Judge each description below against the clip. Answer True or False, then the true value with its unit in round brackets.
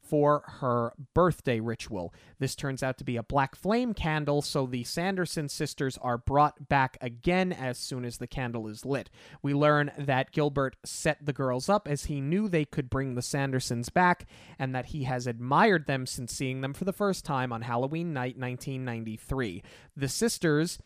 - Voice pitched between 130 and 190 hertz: True (140 Hz)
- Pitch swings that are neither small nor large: True (3.4 semitones)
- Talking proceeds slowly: False (185 wpm)